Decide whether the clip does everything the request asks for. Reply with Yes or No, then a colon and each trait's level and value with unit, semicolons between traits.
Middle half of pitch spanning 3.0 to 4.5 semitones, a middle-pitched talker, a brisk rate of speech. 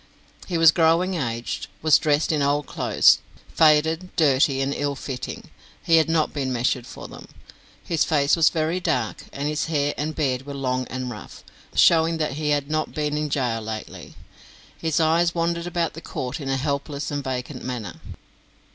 No: average, 3.3 semitones; medium, 145 Hz; average, 180 wpm